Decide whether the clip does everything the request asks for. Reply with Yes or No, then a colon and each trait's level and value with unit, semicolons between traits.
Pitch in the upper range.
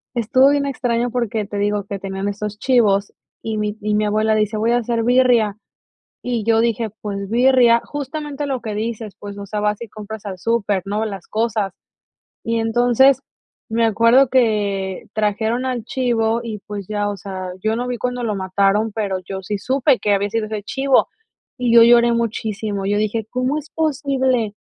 Yes: high, 220 Hz